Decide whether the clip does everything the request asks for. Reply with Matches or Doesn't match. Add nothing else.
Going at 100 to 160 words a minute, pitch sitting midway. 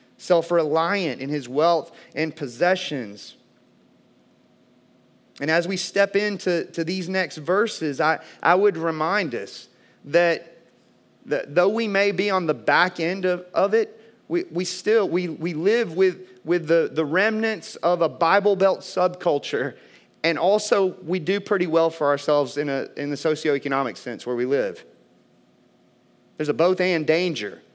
Matches